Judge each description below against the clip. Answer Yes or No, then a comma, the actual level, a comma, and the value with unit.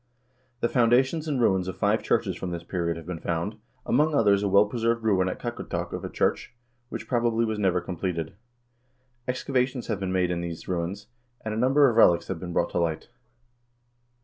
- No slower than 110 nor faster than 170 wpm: No, average, 200 wpm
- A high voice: No, low, 100 Hz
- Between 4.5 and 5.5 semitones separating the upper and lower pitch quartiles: Yes, average, 5.1 semitones